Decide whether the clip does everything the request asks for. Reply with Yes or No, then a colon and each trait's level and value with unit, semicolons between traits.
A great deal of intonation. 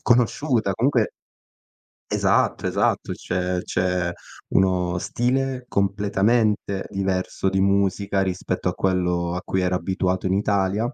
No: narrow, 2.4 semitones